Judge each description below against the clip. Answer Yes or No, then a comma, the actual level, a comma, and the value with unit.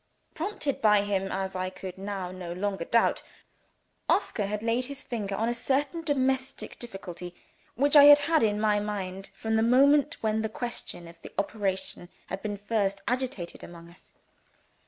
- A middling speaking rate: Yes, average, 170 wpm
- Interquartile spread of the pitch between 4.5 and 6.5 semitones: Yes, average, 5.0 semitones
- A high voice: Yes, high, 210 Hz